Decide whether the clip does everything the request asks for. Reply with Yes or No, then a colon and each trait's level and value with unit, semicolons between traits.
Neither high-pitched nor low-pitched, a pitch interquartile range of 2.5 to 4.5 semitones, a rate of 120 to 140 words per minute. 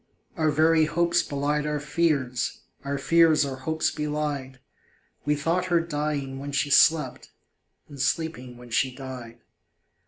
Yes: medium, 150 Hz; average, 3.0 semitones; slow, 135 wpm